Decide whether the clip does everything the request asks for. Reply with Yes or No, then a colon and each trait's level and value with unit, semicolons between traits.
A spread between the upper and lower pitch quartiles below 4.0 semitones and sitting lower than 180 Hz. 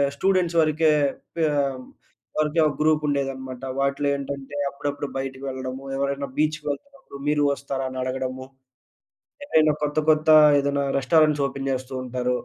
Yes: narrow, 2.4 semitones; medium, 140 Hz